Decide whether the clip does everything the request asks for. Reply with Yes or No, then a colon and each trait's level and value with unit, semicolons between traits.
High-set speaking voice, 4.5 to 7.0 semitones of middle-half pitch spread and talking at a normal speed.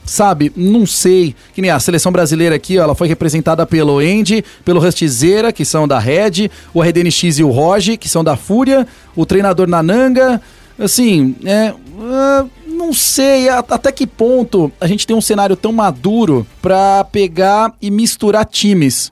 Yes: high, 195 Hz; average, 5.2 semitones; average, 165 wpm